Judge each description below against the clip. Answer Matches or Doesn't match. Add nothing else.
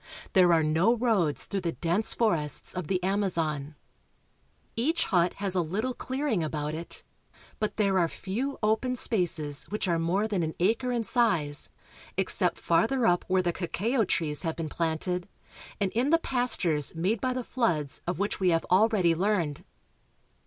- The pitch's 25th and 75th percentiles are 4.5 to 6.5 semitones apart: Matches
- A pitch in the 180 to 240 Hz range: Matches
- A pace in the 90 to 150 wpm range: Doesn't match